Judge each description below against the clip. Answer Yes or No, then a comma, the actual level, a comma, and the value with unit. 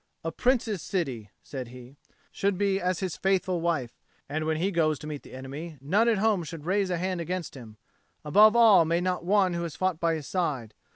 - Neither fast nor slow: No, fast, 215 wpm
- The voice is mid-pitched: Yes, medium, 170 Hz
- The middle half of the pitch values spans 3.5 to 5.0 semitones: Yes, average, 4.3 semitones